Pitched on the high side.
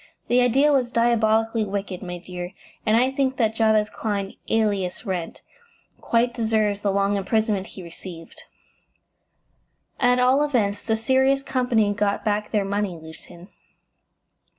Yes: high, 215 Hz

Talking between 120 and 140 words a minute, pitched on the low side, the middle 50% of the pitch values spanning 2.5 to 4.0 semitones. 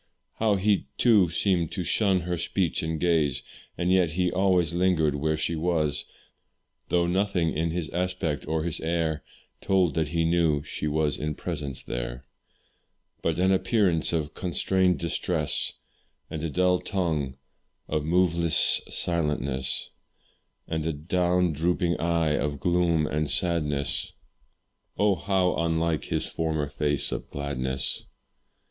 Yes: slow, 135 wpm; very low, 85 Hz; average, 2.8 semitones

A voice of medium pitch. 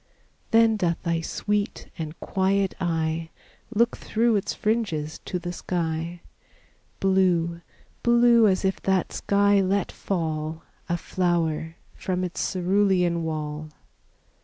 Yes: medium, 180 Hz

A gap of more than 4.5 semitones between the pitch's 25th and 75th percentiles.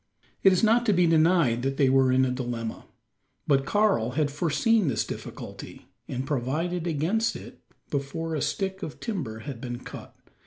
Yes: wide, 5.6 semitones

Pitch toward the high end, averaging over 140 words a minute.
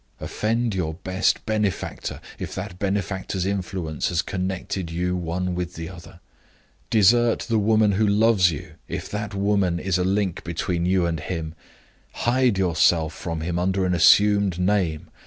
No: very low, 95 Hz; average, 155 wpm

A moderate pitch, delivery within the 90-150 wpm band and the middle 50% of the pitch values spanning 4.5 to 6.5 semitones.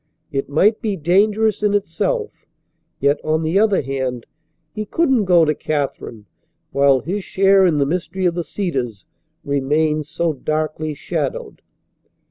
Yes: medium, 160 Hz; average, 140 wpm; wide, 5.6 semitones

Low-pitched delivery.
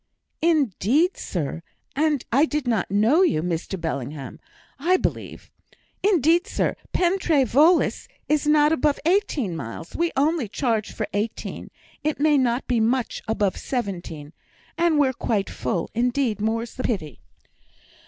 No: very high, 250 Hz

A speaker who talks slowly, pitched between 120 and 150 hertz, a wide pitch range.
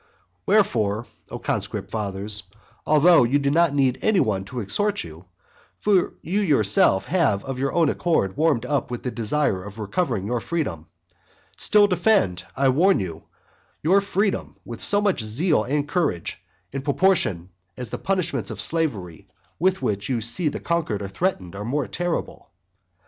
No: average, 170 wpm; low, 135 Hz; wide, 8.9 semitones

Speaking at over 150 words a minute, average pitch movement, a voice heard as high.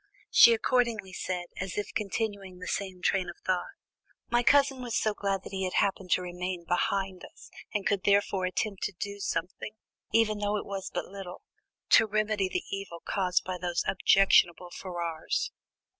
No: average, 175 wpm; narrow, 2.3 semitones; high, 195 Hz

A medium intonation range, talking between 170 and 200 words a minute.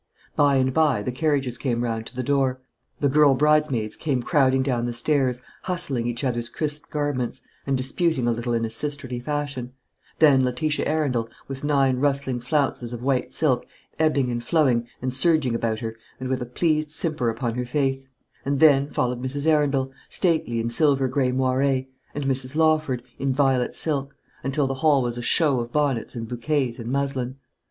Yes: average, 3.0 semitones; average, 180 wpm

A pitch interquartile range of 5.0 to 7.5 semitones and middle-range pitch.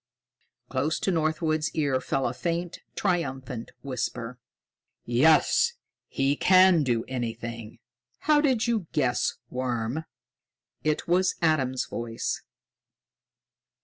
Yes: wide, 5.5 semitones; medium, 145 Hz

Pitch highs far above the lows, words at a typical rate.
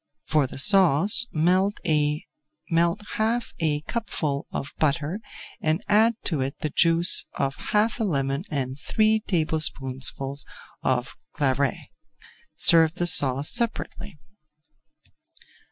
No: wide, 6.4 semitones; slow, 105 wpm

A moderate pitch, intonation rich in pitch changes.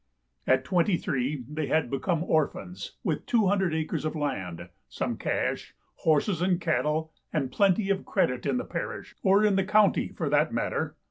No: medium, 160 Hz; average, 4.6 semitones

